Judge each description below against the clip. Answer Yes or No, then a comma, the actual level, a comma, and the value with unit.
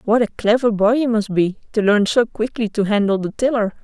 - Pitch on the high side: Yes, high, 215 Hz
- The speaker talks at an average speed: No, fast, 235 wpm